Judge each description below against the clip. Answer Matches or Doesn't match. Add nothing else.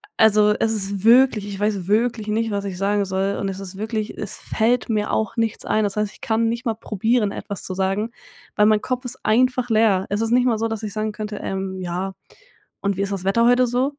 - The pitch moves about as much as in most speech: Doesn't match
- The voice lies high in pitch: Matches